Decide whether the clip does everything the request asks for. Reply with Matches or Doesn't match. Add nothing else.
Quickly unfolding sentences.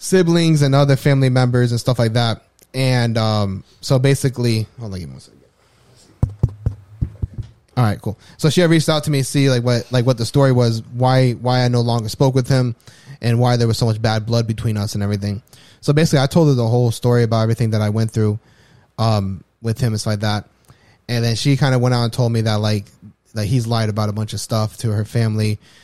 Matches